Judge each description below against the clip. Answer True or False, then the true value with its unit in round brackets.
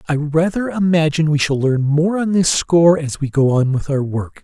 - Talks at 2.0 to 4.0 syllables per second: False (5.2 syllables/s)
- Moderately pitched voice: True (155 Hz)